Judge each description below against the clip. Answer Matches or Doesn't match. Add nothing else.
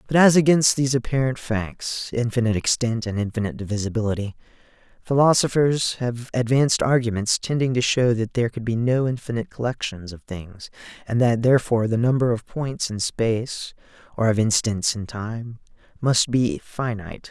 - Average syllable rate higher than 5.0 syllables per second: Matches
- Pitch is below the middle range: Matches